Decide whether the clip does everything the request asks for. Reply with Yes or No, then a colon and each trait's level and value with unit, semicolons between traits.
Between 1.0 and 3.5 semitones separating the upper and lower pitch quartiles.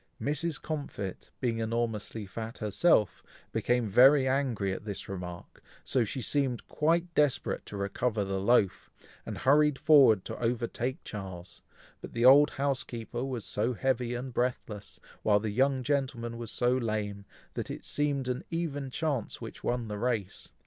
No: average, 4.2 semitones